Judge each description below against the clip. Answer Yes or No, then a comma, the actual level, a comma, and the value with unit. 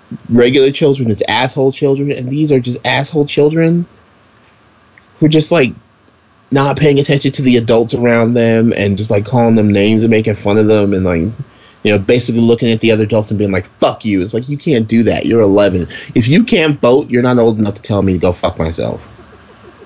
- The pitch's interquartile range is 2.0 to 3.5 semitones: No, average, 4.5 semitones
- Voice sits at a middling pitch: No, low, 115 Hz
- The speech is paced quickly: Yes, fast, 220 wpm